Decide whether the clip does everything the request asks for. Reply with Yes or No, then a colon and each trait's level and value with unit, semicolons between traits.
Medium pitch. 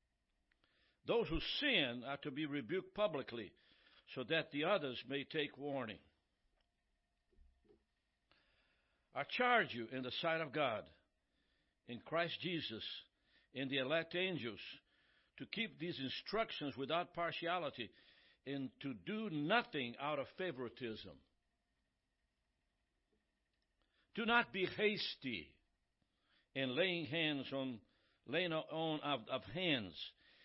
Yes: medium, 145 Hz